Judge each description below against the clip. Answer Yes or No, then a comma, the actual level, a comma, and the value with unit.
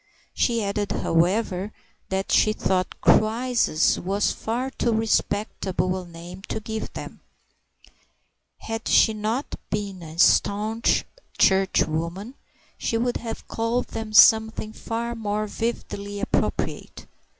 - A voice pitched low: No, high, 215 Hz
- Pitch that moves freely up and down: No, average, 2.9 semitones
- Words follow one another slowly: Yes, slow, 115 wpm